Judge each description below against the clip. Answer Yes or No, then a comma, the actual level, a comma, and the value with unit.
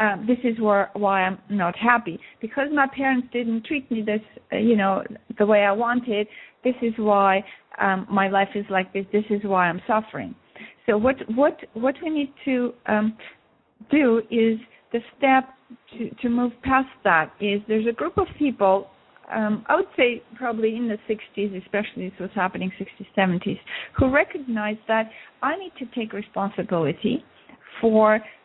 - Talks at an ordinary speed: Yes, average, 175 wpm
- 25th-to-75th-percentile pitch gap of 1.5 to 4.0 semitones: Yes, average, 3.5 semitones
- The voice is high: Yes, high, 220 Hz